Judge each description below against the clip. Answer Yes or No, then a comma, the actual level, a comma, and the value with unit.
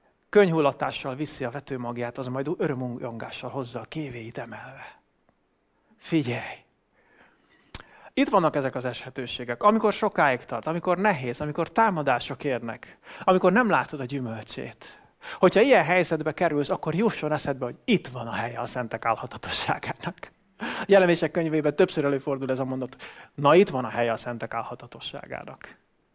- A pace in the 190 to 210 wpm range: No, average, 140 wpm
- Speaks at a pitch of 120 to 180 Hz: Yes, medium, 140 Hz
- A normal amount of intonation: No, wide, 5.9 semitones